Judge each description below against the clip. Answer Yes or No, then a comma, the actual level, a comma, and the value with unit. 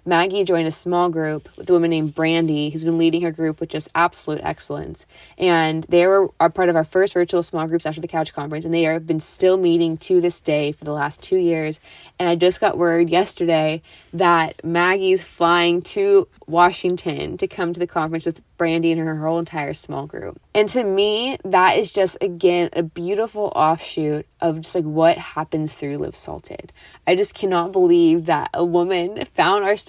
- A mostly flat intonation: Yes, narrow, 2.1 semitones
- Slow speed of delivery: No, average, 200 wpm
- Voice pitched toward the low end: No, medium, 170 Hz